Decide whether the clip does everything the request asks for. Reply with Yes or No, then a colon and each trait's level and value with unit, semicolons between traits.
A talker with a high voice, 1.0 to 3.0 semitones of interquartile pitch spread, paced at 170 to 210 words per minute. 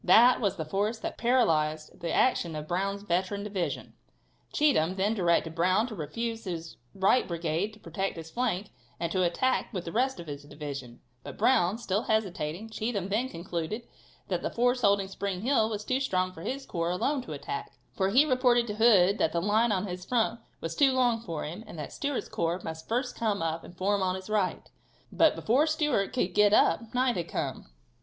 No: high, 200 Hz; wide, 5.4 semitones; average, 200 wpm